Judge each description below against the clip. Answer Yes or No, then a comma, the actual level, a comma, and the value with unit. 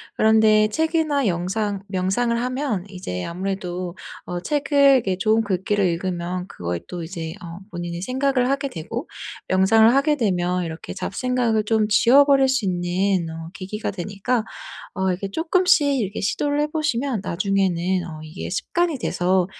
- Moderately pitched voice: No, high, 200 Hz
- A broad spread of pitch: Yes, wide, 5.8 semitones